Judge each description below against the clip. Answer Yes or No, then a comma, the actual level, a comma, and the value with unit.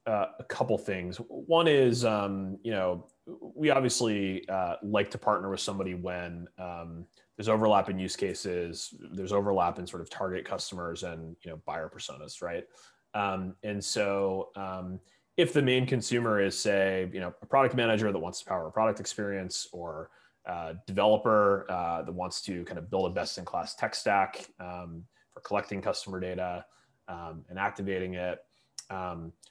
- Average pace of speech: Yes, average, 175 wpm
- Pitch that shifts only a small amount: No, average, 3.0 semitones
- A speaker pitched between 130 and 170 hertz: No, very low, 95 Hz